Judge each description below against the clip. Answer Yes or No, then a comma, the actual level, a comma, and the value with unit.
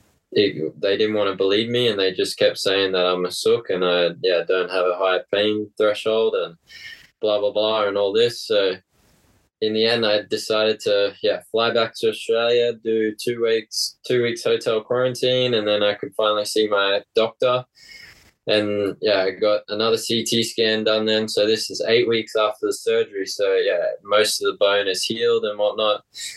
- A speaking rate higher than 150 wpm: Yes, average, 195 wpm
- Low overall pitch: Yes, low, 115 Hz